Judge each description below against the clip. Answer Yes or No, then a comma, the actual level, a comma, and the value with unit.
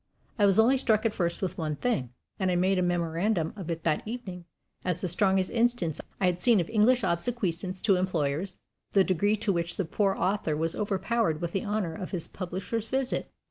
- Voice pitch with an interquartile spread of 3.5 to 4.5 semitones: Yes, average, 3.8 semitones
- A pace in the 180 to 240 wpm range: Yes, fast, 205 wpm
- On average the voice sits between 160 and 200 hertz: Yes, medium, 185 Hz